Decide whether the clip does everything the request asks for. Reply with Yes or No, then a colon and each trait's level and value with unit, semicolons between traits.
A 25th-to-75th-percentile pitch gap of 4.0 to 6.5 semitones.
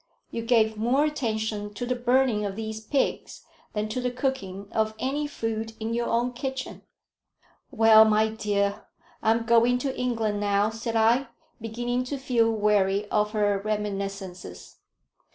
No: average, 2.7 semitones